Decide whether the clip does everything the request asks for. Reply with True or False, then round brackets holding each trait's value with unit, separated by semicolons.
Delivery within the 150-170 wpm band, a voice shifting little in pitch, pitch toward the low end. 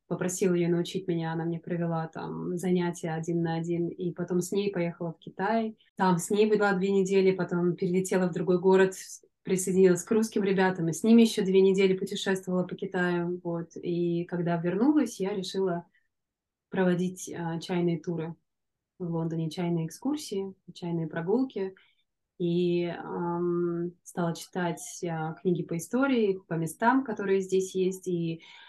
False (155 wpm; 2.1 semitones; 180 Hz)